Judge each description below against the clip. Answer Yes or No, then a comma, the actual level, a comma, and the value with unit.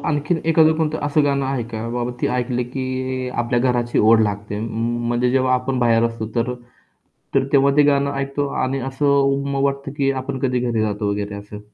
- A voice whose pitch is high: No, low, 130 Hz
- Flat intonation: No, average, 3.1 semitones